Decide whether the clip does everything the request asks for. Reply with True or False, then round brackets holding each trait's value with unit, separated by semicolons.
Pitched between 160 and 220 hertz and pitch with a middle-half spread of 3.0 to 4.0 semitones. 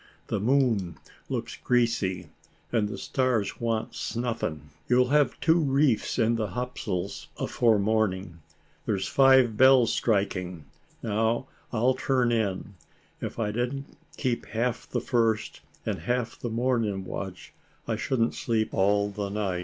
False (115 Hz; 3.5 semitones)